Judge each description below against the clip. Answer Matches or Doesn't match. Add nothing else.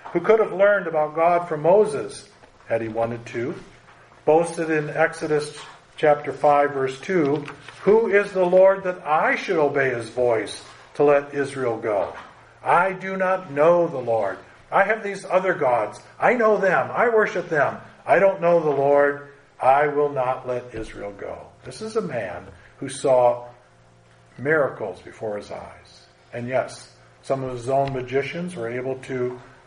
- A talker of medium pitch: Matches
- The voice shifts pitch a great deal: Matches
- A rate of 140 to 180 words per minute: Matches